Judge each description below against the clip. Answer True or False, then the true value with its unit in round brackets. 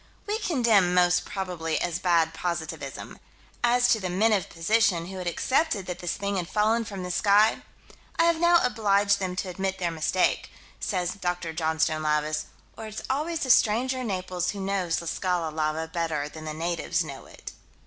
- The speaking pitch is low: False (185 Hz)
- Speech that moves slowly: False (185 wpm)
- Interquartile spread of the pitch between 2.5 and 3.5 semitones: False (4.3 semitones)